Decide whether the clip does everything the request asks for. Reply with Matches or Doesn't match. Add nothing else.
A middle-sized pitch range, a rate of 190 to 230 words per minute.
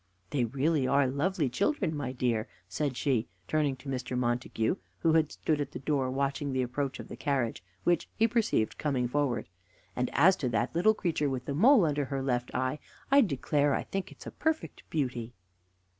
Matches